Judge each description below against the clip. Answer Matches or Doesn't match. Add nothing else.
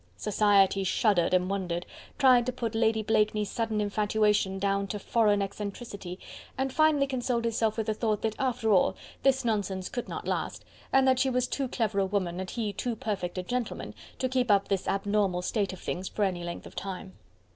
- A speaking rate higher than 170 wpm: Matches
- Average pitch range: Matches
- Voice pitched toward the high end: Matches